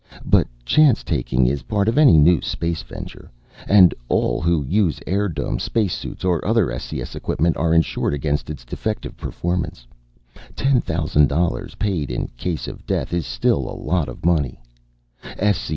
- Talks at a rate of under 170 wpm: Yes, average, 150 wpm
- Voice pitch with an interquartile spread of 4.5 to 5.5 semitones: Yes, average, 5.2 semitones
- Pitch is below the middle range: Yes, very low, 85 Hz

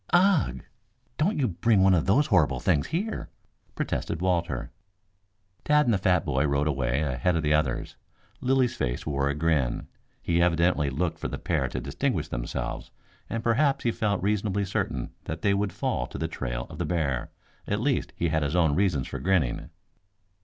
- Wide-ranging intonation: Yes, wide, 6.3 semitones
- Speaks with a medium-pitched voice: No, very low, 85 Hz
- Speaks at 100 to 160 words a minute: No, average, 180 wpm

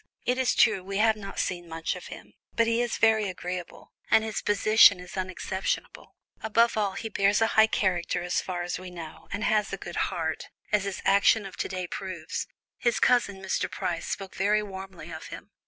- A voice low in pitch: No, high, 195 Hz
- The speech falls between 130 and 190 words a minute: No, fast, 205 wpm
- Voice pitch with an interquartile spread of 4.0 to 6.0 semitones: No, average, 3.0 semitones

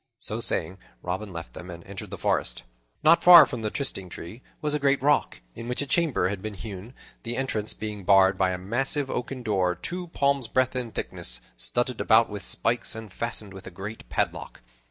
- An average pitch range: No, wide, 5.7 semitones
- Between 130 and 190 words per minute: No, average, 200 wpm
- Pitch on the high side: No, low, 110 Hz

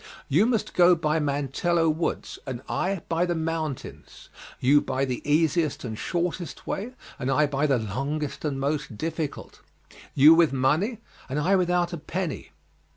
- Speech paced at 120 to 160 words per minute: Yes, average, 155 wpm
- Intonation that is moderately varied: Yes, average, 4.0 semitones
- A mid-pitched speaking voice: Yes, medium, 155 Hz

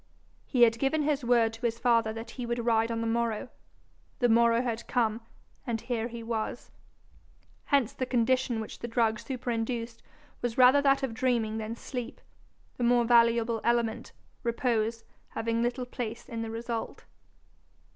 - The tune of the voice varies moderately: No, narrow, 1.4 semitones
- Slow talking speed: No, average, 160 wpm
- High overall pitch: Yes, high, 235 Hz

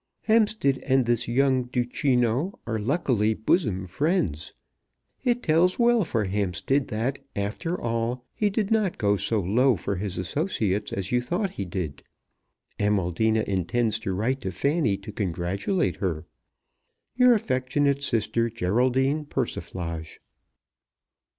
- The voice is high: No, low, 120 Hz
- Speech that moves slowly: Yes, slow, 125 wpm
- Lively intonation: Yes, wide, 6.1 semitones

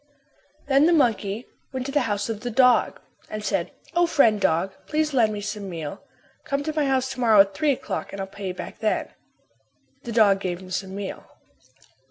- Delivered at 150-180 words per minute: No, fast, 205 wpm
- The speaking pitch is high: Yes, high, 220 Hz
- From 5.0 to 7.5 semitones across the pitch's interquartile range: Yes, wide, 5.4 semitones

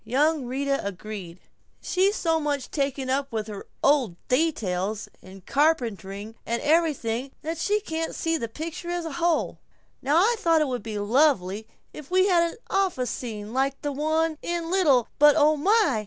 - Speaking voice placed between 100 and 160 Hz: No, very high, 285 Hz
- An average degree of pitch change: No, wide, 6.2 semitones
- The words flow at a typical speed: Yes, average, 170 wpm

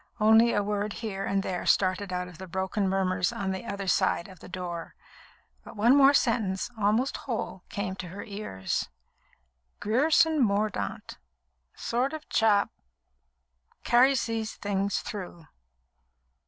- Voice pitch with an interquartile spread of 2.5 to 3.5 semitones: Yes, average, 3.2 semitones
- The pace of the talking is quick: No, average, 140 wpm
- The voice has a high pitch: Yes, high, 200 Hz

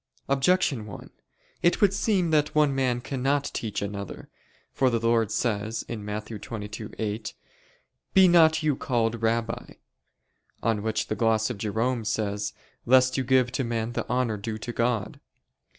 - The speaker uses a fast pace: No, average, 150 wpm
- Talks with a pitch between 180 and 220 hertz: No, low, 115 Hz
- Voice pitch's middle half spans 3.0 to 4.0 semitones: Yes, average, 3.5 semitones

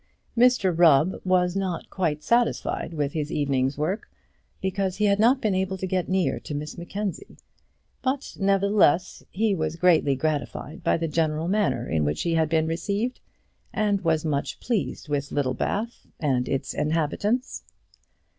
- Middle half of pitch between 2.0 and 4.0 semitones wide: No, average, 4.7 semitones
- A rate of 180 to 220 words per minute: No, average, 155 wpm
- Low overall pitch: No, medium, 170 Hz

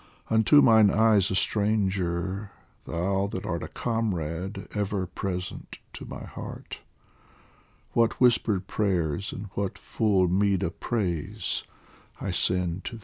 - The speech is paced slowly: Yes, slow, 130 wpm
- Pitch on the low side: Yes, low, 100 Hz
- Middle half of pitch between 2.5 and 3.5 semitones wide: Yes, average, 2.9 semitones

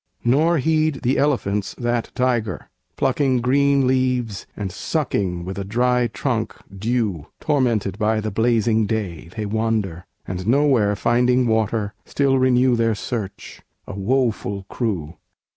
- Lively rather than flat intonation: No, average, 3.9 semitones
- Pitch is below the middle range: Yes, low, 115 Hz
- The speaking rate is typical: No, slow, 130 wpm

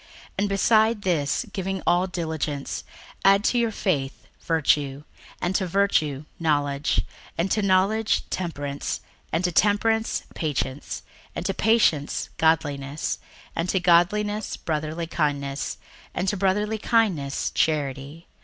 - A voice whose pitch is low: No, medium, 170 Hz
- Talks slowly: Yes, slow, 130 wpm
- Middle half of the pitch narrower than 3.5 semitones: No, wide, 5.4 semitones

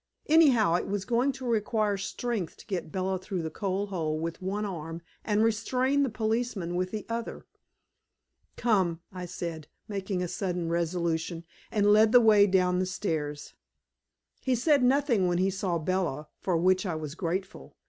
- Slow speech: No, average, 170 wpm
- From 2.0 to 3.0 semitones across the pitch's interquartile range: No, average, 4.2 semitones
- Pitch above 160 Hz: Yes, high, 190 Hz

